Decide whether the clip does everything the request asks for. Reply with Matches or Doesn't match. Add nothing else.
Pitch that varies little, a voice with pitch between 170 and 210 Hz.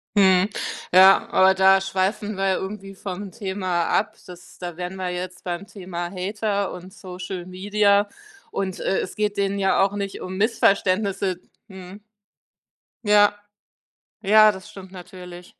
Matches